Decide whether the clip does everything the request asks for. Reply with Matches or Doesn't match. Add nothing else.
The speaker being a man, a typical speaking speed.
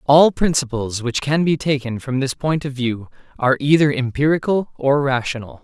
Matches